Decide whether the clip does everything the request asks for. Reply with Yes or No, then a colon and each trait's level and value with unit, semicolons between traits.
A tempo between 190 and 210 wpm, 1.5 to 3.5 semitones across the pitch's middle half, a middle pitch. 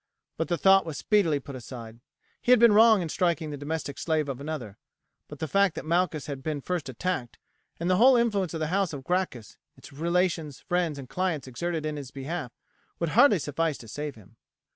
No: fast, 205 wpm; average, 4.5 semitones; medium, 160 Hz